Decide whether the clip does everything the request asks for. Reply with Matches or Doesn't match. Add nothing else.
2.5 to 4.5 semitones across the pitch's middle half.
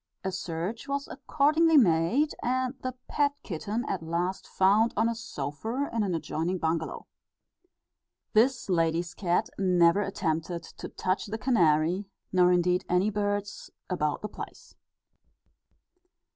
Doesn't match